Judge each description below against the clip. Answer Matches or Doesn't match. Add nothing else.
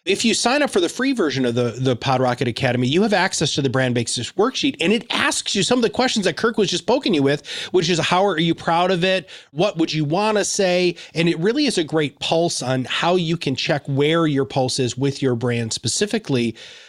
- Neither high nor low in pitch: Matches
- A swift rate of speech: Matches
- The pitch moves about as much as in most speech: Doesn't match